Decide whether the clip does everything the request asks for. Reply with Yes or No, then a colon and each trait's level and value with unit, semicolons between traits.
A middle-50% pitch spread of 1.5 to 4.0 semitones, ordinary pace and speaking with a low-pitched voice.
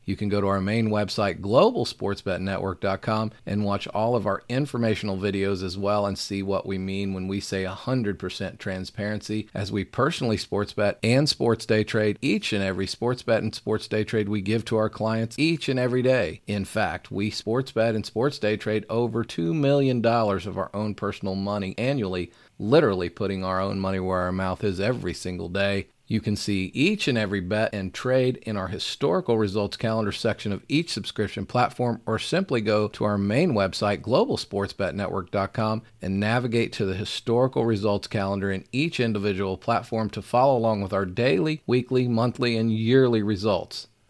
Yes: average, 2.9 semitones; average, 180 wpm; low, 105 Hz